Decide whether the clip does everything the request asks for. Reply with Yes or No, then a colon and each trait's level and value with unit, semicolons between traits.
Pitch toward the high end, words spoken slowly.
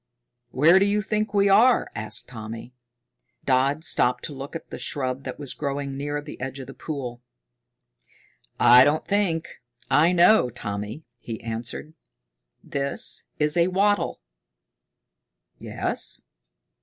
No: medium, 140 Hz; slow, 130 wpm